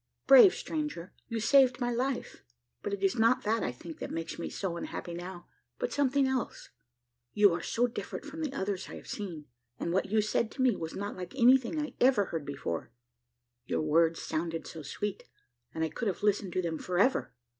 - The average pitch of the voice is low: No, high, 205 Hz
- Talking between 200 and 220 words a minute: Yes, fast, 205 wpm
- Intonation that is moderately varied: No, wide, 6.9 semitones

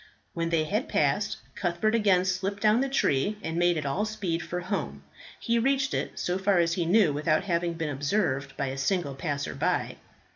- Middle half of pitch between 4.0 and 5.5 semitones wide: Yes, average, 4.6 semitones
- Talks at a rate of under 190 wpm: No, average, 195 wpm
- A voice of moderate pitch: Yes, medium, 175 Hz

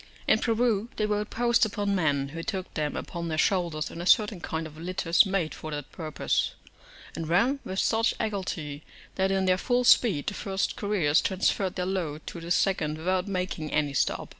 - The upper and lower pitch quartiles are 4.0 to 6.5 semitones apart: Yes, average, 4.3 semitones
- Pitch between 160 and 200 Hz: Yes, medium, 185 Hz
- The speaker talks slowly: No, average, 190 wpm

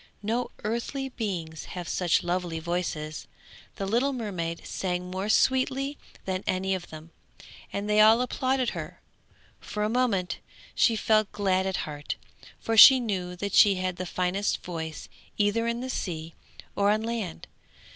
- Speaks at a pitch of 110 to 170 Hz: No, high, 200 Hz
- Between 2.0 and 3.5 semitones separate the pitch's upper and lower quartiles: No, average, 4.3 semitones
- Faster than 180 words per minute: No, average, 155 wpm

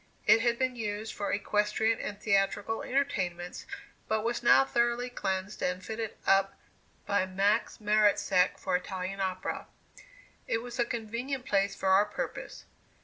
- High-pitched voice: Yes, high, 210 Hz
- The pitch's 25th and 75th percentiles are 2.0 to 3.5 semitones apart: Yes, average, 3.2 semitones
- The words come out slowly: No, average, 145 wpm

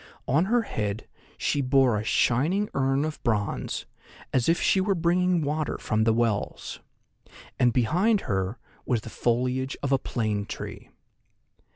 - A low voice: Yes, low, 130 Hz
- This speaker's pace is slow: No, average, 150 wpm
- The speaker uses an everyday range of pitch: No, wide, 6.5 semitones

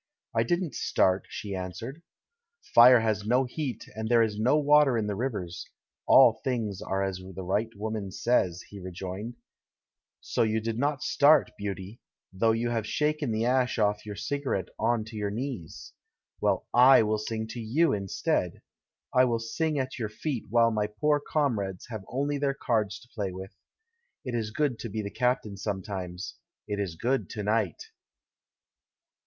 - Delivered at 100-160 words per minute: No, average, 175 wpm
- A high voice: No, low, 110 Hz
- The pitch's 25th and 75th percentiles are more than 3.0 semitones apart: Yes, average, 3.9 semitones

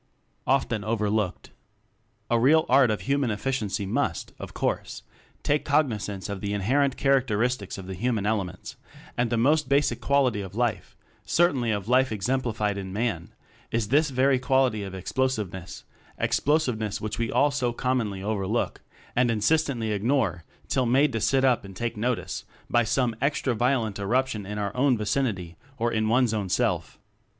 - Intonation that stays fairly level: No, average, 4.2 semitones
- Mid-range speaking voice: No, low, 115 Hz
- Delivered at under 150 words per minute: No, average, 165 wpm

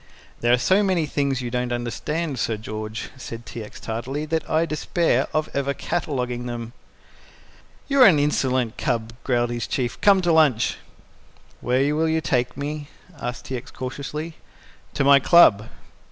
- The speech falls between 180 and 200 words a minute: No, average, 165 wpm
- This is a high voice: No, low, 135 Hz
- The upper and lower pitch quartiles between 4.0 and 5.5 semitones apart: Yes, average, 4.3 semitones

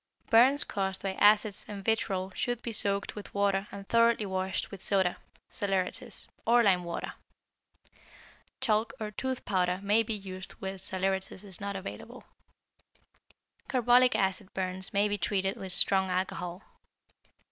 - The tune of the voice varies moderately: No, narrow, 2.1 semitones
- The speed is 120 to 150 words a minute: Yes, average, 140 wpm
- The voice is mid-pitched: No, high, 195 Hz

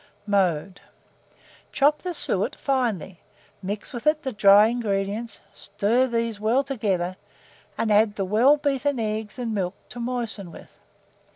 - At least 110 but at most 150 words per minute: Yes, average, 145 wpm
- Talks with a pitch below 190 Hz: No, high, 220 Hz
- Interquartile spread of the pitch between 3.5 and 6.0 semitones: Yes, average, 4.0 semitones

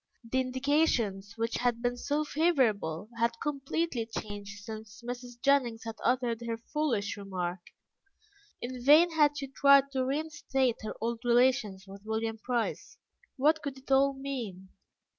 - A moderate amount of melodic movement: Yes, average, 3.9 semitones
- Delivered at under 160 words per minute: Yes, average, 140 wpm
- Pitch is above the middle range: Yes, high, 245 Hz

